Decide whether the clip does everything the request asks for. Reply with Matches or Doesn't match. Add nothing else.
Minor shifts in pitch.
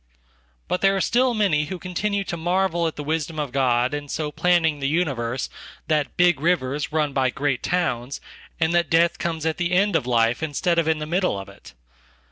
Doesn't match